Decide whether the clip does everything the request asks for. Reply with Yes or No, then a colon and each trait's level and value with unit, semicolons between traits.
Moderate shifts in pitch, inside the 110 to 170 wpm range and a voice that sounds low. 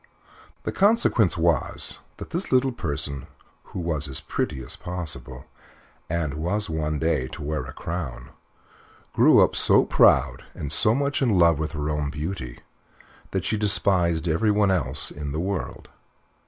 Yes: average, 4.8 semitones; average, 155 wpm; very low, 85 Hz